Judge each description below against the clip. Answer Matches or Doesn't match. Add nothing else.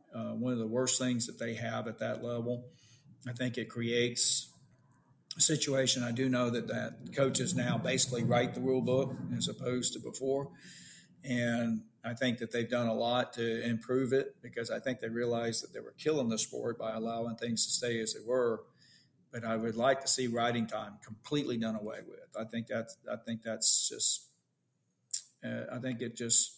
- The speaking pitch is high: Doesn't match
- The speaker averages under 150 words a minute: Doesn't match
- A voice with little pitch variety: Matches